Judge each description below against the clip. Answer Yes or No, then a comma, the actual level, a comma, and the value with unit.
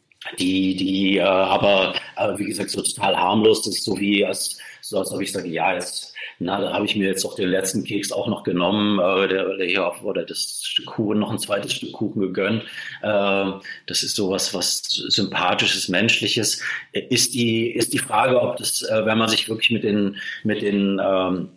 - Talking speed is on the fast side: Yes, fast, 200 wpm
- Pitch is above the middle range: No, low, 105 Hz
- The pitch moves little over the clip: Yes, narrow, 2.1 semitones